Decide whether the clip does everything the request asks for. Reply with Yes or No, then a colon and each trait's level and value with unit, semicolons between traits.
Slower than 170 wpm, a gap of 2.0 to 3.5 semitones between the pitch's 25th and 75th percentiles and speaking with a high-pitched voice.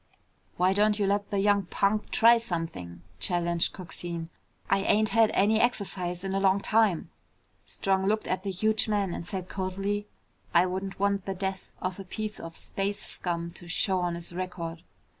No: average, 180 wpm; narrow, 2.5 semitones; high, 195 Hz